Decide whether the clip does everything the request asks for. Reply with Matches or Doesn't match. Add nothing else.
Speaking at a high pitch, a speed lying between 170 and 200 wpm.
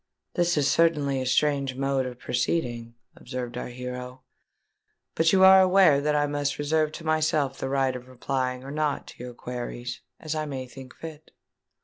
Doesn't match